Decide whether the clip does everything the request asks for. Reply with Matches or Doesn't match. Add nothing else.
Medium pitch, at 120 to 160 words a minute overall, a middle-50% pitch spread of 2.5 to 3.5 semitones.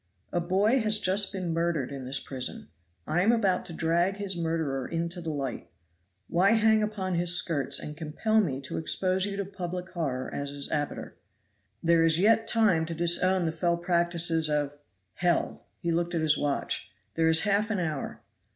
Doesn't match